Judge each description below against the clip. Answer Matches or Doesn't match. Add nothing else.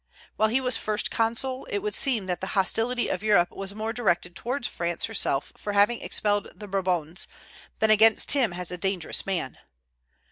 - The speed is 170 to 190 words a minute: Matches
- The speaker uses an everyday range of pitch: Matches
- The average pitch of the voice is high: Matches